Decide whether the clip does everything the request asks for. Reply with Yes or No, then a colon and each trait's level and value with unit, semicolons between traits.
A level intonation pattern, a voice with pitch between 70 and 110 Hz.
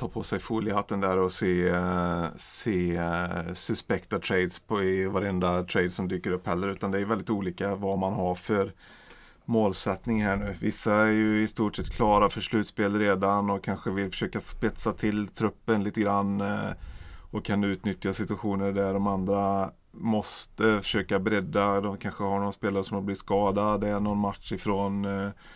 Yes: narrow, 1.7 semitones; low, 100 Hz